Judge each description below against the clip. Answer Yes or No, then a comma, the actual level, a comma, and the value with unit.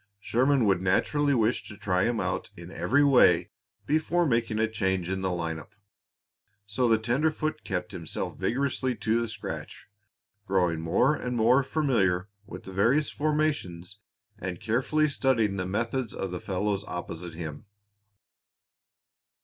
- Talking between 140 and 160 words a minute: Yes, average, 145 wpm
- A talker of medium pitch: No, low, 110 Hz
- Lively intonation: Yes, wide, 6.1 semitones